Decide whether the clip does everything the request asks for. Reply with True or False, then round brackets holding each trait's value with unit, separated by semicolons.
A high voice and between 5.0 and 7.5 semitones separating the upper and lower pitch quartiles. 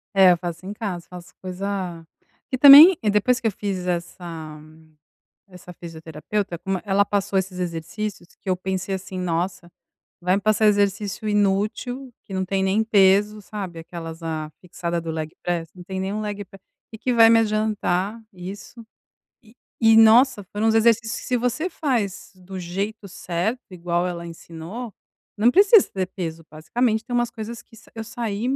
False (195 Hz; 3.8 semitones)